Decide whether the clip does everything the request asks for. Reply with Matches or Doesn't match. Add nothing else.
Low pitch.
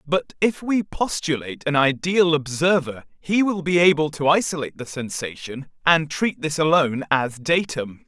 Doesn't match